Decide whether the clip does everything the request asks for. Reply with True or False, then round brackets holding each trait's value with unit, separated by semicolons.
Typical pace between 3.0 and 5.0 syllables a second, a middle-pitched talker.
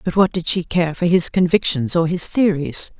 True (4.9 syllables/s; 175 Hz)